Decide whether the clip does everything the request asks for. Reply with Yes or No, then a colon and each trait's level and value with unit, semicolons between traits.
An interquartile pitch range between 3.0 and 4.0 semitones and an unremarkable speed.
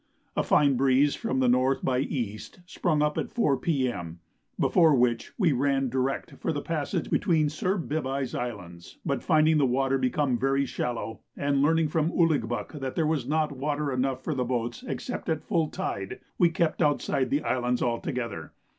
Yes: average, 3.6 semitones; average, 170 wpm